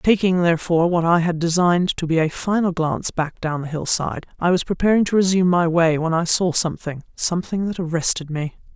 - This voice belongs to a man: No, female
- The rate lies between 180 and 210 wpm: Yes, average, 200 wpm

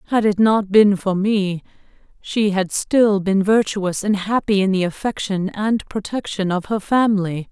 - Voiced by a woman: Yes, female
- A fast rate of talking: No, average, 170 wpm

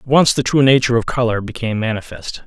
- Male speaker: Yes, male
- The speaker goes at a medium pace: No, fast, 220 wpm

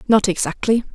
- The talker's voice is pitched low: No, high, 215 Hz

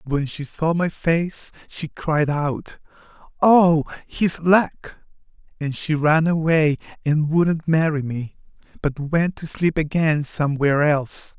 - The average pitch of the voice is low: No, medium, 155 Hz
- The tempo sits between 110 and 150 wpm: Yes, slow, 135 wpm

